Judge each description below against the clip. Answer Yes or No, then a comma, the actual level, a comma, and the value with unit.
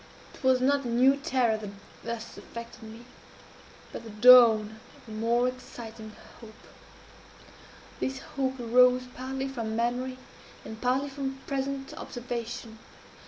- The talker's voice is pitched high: Yes, high, 245 Hz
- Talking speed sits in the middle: No, slow, 130 wpm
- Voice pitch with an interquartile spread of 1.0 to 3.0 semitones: Yes, narrow, 2.6 semitones